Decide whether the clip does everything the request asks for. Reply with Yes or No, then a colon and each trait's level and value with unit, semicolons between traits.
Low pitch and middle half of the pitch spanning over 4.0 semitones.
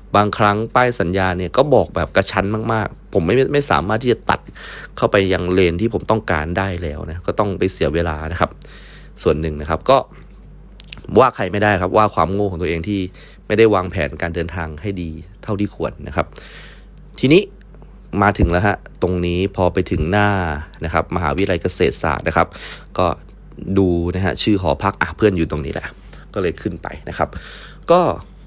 No: very low, 95 Hz; average, 3.4 semitones